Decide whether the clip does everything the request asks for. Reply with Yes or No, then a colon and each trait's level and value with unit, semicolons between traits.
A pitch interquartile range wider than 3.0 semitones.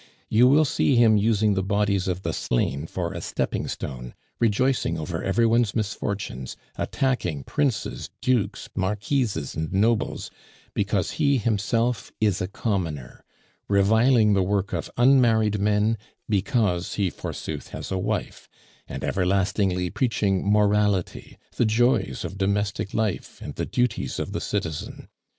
Yes: average, 3.4 semitones